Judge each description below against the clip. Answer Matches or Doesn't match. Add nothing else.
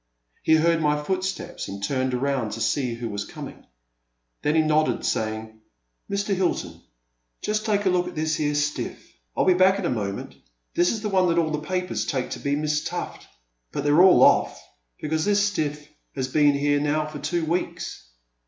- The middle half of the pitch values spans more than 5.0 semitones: Doesn't match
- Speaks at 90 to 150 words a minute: Doesn't match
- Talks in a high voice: Doesn't match